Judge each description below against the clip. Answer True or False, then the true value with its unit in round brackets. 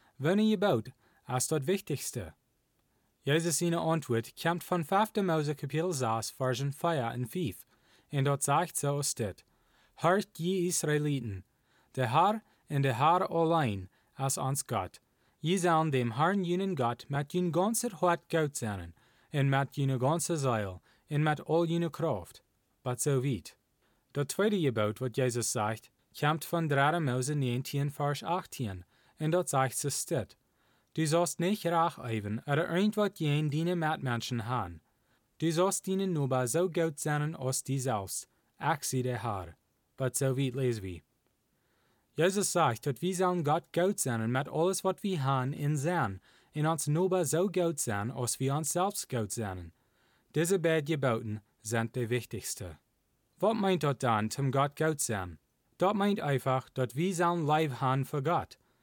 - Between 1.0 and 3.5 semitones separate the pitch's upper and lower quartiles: False (5.3 semitones)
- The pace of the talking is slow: False (165 wpm)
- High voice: False (140 Hz)